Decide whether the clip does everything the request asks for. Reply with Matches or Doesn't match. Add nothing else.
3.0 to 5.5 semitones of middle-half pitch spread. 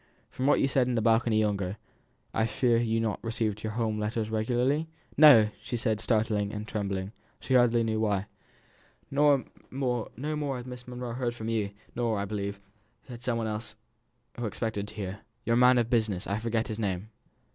Doesn't match